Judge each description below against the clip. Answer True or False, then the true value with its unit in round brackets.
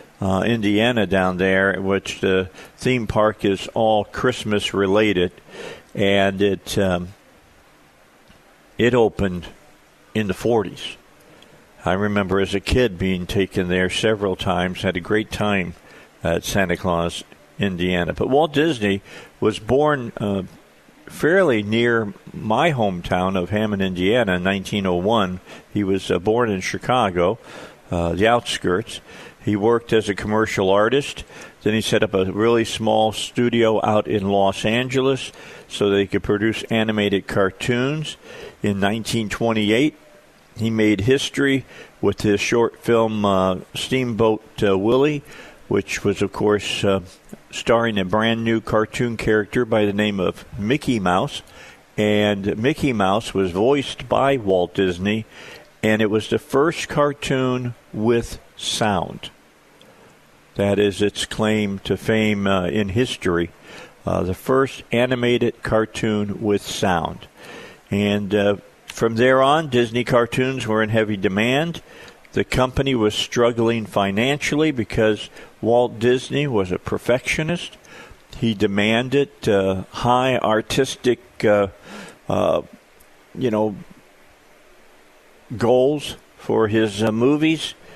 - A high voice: False (110 Hz)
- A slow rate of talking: True (125 wpm)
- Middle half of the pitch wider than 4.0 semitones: False (3.4 semitones)